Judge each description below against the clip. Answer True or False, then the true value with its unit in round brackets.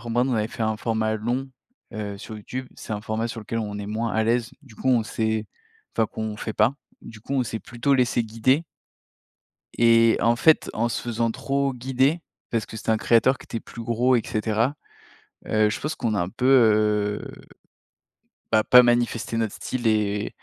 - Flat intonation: True (2.1 semitones)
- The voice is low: True (115 Hz)